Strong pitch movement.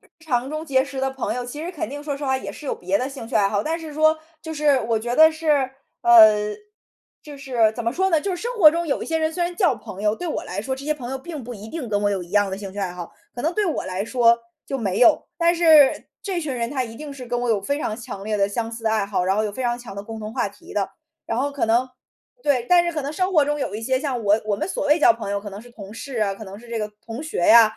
Yes: wide, 5.9 semitones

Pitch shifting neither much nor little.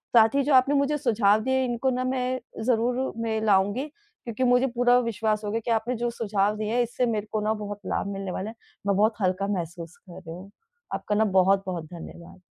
Yes: average, 4.0 semitones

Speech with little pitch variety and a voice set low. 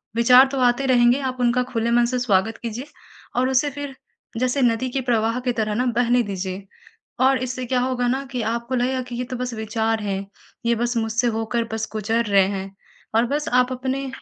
No: narrow, 2.2 semitones; high, 240 Hz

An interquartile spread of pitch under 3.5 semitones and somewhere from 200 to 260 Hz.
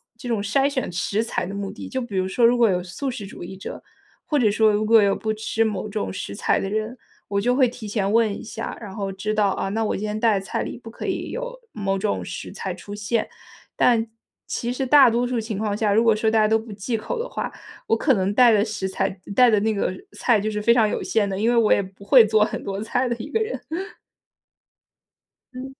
Yes: average, 2.8 semitones; high, 220 Hz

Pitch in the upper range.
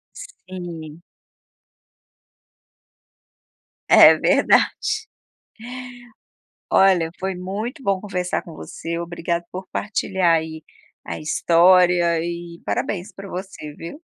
No: medium, 180 Hz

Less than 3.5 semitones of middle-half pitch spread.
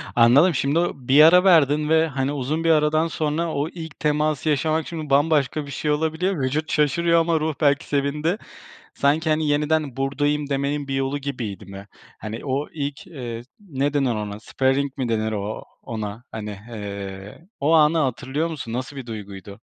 No: average, 3.8 semitones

